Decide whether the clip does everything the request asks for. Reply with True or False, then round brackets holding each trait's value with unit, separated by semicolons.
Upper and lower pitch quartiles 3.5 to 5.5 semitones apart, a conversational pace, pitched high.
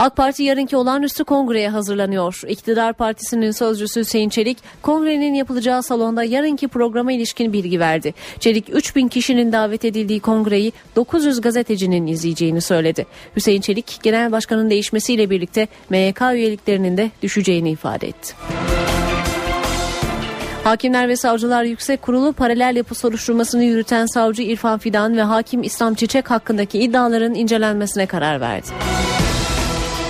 False (2.9 semitones; 125 wpm; 225 Hz)